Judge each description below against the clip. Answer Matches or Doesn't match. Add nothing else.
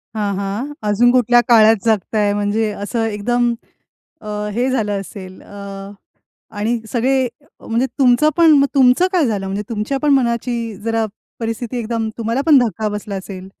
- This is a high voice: Matches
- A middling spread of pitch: Matches